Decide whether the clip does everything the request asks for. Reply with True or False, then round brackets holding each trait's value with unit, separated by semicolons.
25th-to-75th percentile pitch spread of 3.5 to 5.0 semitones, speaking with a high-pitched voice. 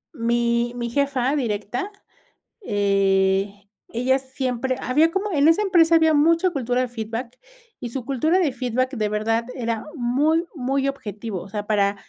True (4.1 semitones; 250 Hz)